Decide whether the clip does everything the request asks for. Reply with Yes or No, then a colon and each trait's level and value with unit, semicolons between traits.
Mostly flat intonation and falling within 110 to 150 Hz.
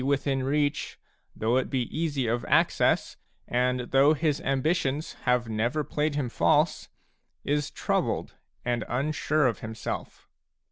No: average, 3.3 semitones; low, 135 Hz